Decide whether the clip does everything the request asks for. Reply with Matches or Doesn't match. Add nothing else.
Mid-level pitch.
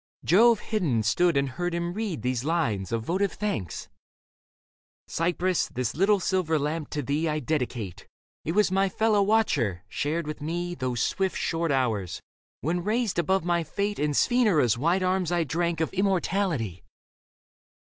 Matches